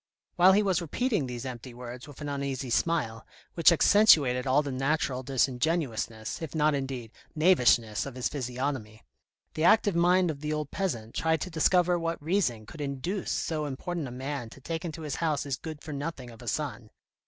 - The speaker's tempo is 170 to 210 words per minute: Yes, average, 190 wpm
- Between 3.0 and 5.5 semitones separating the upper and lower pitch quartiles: Yes, average, 4.7 semitones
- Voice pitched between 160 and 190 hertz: No, medium, 145 Hz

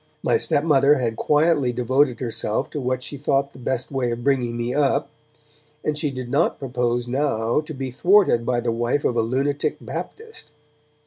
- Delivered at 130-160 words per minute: No, average, 180 wpm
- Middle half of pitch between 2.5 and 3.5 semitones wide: Yes, average, 3.2 semitones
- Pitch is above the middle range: No, low, 130 Hz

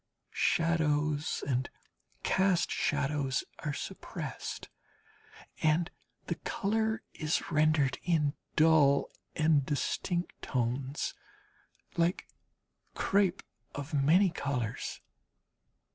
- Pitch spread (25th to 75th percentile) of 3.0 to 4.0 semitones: Yes, average, 3.4 semitones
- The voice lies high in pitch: No, medium, 155 Hz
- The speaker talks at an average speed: No, slow, 80 wpm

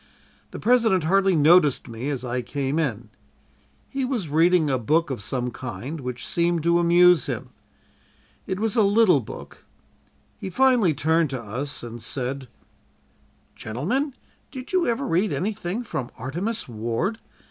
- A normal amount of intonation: No, wide, 7.6 semitones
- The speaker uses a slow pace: No, average, 145 wpm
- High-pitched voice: No, medium, 165 Hz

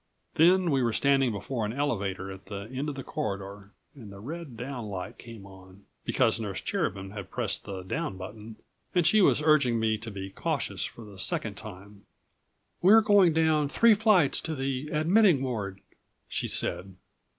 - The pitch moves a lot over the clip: Yes, wide, 7.3 semitones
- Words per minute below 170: No, average, 175 wpm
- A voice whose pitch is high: No, low, 115 Hz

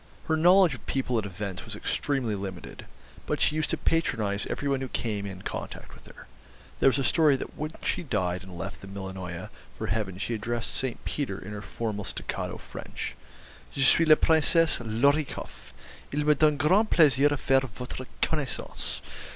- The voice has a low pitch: Yes, low, 125 Hz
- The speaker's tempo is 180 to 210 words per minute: Yes, average, 190 wpm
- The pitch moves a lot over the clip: Yes, wide, 6.7 semitones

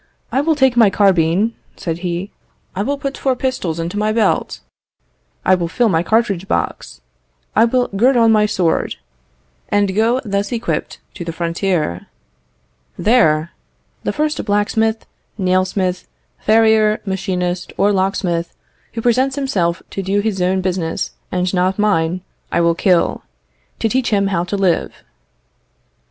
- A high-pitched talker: Yes, high, 195 Hz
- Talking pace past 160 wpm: No, average, 145 wpm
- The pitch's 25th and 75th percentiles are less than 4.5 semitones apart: Yes, average, 3.9 semitones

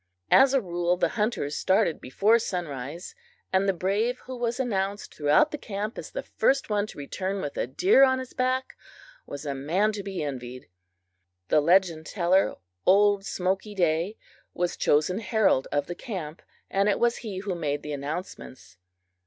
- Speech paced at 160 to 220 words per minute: Yes, average, 170 wpm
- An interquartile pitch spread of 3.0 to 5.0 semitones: No, wide, 5.5 semitones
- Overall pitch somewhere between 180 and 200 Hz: Yes, high, 190 Hz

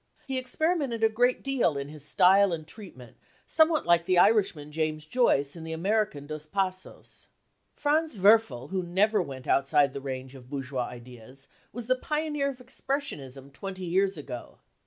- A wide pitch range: Yes, wide, 8.3 semitones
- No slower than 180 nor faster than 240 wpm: No, average, 165 wpm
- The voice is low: No, medium, 180 Hz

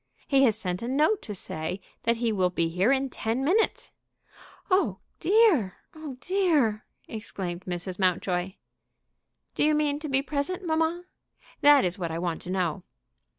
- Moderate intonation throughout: No, wide, 8.7 semitones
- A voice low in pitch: No, high, 235 Hz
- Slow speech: No, average, 160 wpm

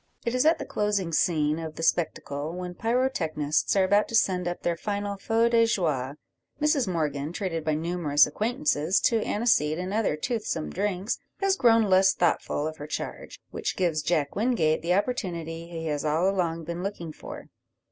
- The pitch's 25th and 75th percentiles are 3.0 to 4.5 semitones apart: No, average, 5.0 semitones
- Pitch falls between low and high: Yes, medium, 180 Hz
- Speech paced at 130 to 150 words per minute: No, average, 180 wpm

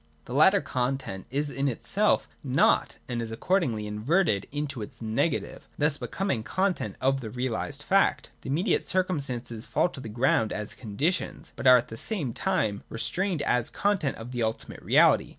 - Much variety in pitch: Yes, wide, 6.2 semitones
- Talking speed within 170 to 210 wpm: Yes, average, 175 wpm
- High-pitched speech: No, low, 130 Hz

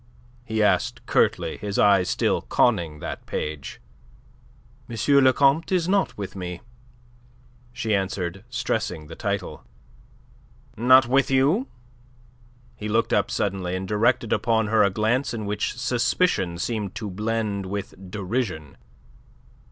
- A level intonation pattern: No, average, 4.1 semitones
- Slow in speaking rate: Yes, slow, 130 wpm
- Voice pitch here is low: Yes, low, 105 Hz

